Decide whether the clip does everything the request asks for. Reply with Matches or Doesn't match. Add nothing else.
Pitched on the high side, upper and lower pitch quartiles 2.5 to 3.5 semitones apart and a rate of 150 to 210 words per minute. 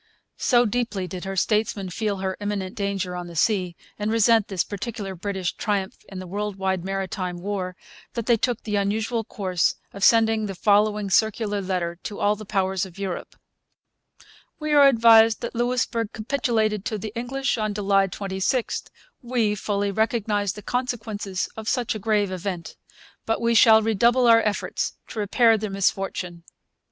Matches